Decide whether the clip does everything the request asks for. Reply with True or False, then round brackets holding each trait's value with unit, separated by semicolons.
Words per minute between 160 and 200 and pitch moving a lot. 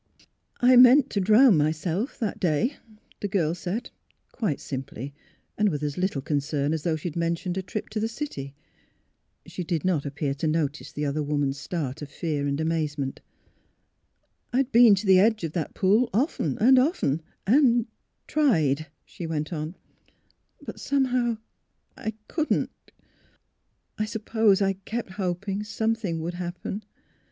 True (170 wpm; 6.5 semitones)